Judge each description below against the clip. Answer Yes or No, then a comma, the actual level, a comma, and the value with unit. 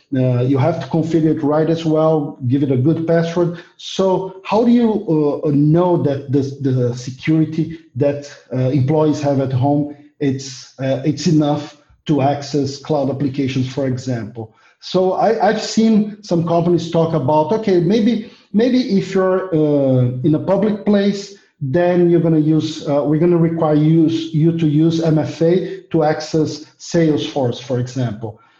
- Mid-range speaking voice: Yes, medium, 155 Hz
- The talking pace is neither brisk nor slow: Yes, average, 165 wpm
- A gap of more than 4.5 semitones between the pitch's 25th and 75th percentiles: No, average, 3.4 semitones